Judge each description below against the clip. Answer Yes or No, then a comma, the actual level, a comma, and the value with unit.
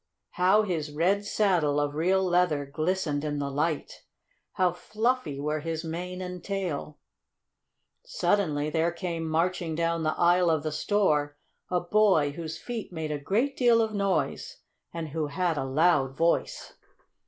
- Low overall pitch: No, medium, 170 Hz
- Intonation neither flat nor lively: Yes, average, 3.8 semitones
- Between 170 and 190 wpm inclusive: No, average, 155 wpm